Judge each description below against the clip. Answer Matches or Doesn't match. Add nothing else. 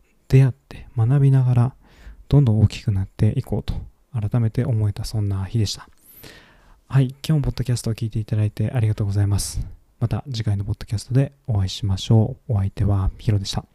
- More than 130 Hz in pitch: Doesn't match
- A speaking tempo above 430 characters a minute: Doesn't match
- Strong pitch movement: Doesn't match